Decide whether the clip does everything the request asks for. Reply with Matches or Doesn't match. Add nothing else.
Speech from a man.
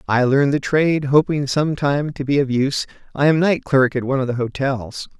Matches